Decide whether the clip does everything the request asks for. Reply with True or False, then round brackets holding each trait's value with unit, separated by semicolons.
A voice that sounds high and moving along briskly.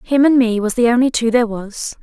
True (235 Hz; 265 wpm)